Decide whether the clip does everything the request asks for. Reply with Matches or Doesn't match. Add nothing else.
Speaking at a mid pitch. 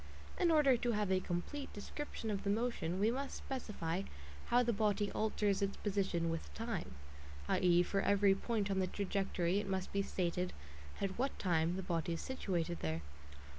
Doesn't match